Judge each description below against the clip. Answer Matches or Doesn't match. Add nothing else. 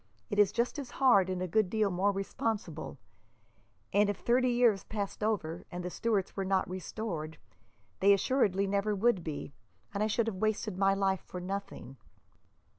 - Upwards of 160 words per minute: Matches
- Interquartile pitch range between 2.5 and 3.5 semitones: Matches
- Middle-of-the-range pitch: Doesn't match